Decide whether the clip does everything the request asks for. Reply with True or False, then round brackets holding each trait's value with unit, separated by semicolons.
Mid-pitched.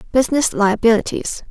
False (230 Hz)